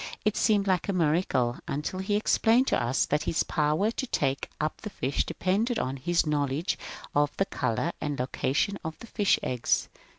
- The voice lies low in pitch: No, medium, 160 Hz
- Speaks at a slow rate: No, average, 185 wpm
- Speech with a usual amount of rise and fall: No, wide, 6.1 semitones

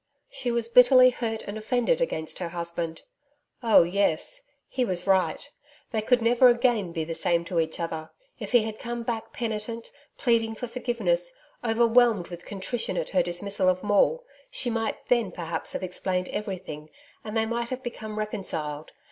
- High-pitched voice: Yes, high, 220 Hz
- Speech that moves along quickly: No, average, 170 wpm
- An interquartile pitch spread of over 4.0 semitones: Yes, average, 5.1 semitones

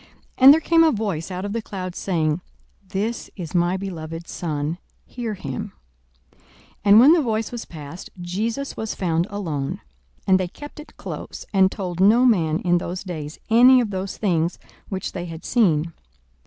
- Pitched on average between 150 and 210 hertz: Yes, high, 190 Hz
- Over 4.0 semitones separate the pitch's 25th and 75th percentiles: Yes, average, 4.8 semitones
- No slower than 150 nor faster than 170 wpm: No, average, 180 wpm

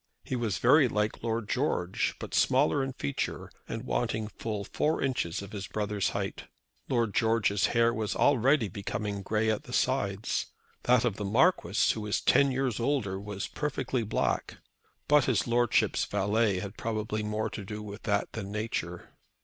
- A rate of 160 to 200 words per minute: Yes, average, 165 wpm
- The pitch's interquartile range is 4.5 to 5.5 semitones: No, average, 3.2 semitones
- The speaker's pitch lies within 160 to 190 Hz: No, low, 110 Hz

